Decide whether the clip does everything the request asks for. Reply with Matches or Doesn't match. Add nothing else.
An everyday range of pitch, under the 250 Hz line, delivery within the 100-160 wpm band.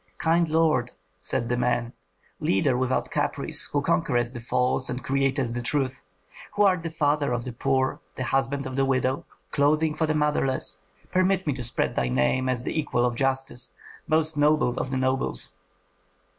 Doesn't match